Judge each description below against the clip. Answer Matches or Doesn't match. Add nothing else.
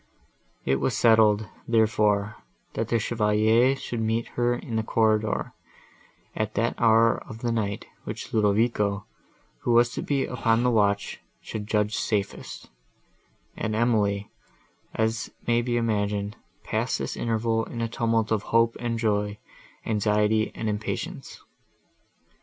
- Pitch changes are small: Matches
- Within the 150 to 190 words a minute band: Doesn't match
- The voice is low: Matches